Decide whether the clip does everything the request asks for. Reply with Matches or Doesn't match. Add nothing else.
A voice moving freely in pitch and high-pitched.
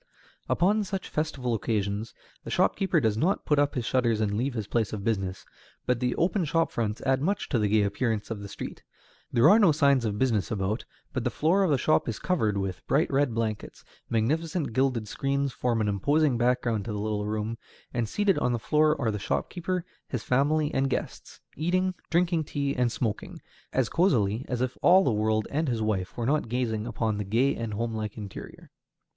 Doesn't match